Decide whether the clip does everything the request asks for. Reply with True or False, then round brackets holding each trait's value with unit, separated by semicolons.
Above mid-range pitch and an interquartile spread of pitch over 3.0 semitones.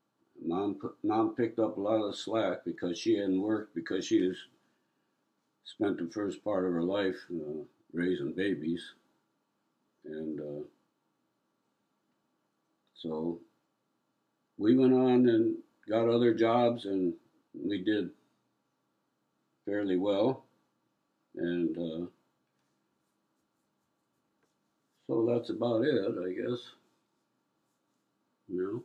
False (100 Hz; 5.4 semitones)